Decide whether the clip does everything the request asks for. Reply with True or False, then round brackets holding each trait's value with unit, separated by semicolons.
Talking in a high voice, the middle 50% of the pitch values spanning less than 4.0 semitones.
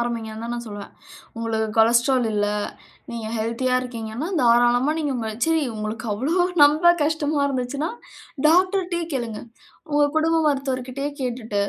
False (250 Hz; 4.4 semitones)